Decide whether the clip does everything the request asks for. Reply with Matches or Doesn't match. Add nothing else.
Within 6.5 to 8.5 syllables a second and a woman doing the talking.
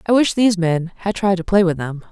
Doesn't match